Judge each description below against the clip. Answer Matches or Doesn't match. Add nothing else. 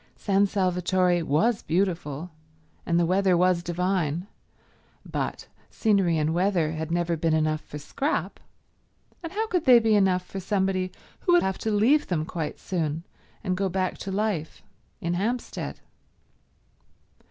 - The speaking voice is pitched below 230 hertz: Matches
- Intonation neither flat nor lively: Matches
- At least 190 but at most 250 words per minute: Doesn't match